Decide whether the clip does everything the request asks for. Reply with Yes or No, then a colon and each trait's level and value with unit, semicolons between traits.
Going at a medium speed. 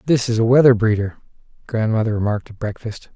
Yes: average, 170 wpm